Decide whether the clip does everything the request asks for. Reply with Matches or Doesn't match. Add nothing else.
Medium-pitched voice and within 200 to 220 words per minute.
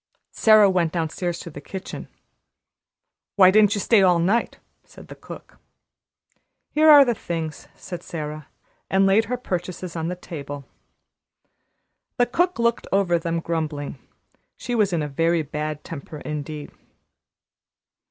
Doesn't match